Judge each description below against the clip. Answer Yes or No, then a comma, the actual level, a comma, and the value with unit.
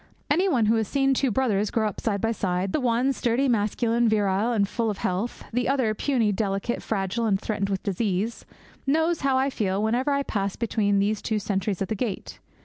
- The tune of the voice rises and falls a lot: No, average, 3.7 semitones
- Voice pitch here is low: No, high, 220 Hz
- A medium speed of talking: No, fast, 210 wpm